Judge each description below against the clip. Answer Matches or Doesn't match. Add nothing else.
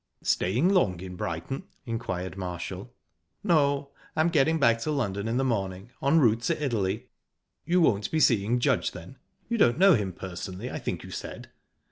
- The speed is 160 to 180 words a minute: Matches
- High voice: Doesn't match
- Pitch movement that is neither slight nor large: Doesn't match